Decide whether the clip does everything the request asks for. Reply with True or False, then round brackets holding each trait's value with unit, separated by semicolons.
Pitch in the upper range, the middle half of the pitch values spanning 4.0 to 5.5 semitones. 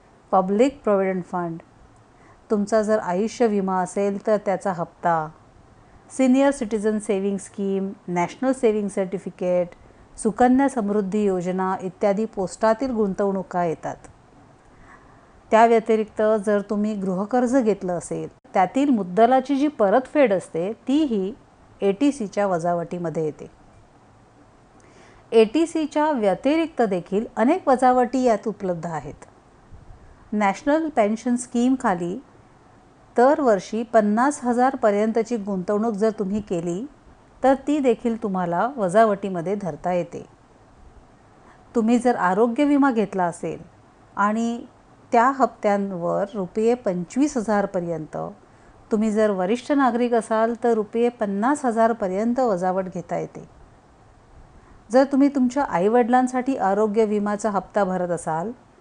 True (215 Hz; 4.3 semitones)